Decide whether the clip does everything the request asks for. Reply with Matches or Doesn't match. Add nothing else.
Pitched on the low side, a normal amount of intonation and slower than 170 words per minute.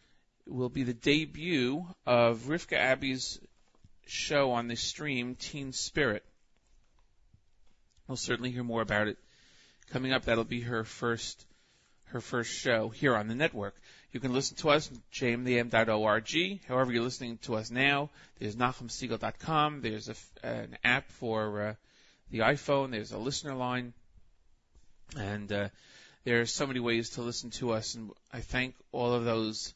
Matches